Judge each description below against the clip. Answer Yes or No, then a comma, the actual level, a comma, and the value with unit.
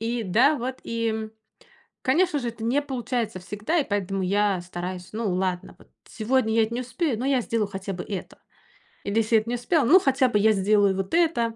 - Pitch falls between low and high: No, high, 225 Hz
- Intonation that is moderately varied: Yes, average, 4.1 semitones